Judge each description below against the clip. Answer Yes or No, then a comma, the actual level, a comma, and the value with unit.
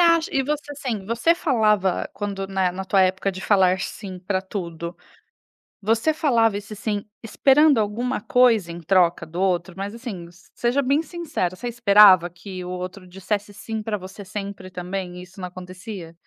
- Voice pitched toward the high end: Yes, high, 200 Hz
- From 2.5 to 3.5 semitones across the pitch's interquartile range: No, average, 4.0 semitones